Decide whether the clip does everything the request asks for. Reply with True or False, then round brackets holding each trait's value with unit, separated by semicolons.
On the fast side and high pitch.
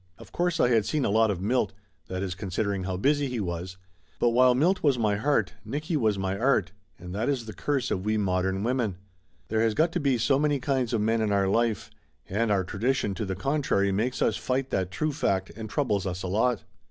False (230 wpm; 110 Hz)